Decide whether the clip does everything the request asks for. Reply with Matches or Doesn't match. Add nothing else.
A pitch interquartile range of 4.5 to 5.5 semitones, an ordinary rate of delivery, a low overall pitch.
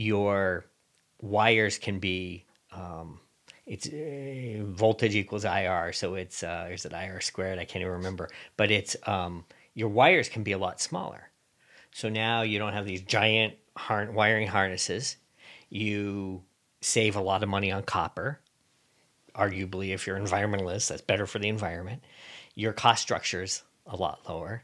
Doesn't match